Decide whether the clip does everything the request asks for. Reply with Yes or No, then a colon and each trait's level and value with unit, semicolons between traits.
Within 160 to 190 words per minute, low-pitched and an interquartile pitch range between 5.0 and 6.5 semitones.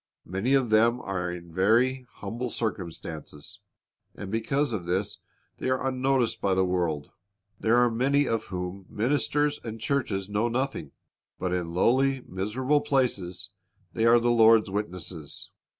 No: average, 145 wpm; low, 110 Hz; wide, 5.6 semitones